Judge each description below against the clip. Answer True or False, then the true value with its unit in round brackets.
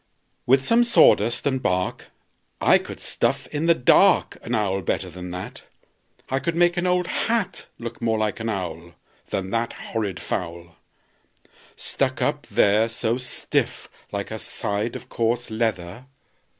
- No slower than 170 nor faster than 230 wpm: False (150 wpm)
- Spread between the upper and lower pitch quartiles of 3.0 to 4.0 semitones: False (5.5 semitones)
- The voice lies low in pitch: True (115 Hz)